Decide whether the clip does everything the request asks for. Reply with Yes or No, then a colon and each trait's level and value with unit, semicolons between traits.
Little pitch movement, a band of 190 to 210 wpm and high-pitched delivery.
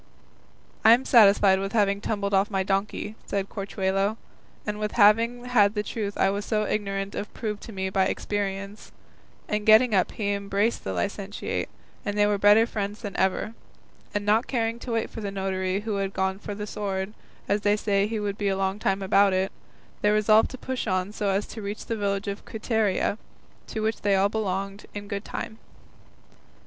Yes: narrow, 1.5 semitones; average, 195 wpm; high, 205 Hz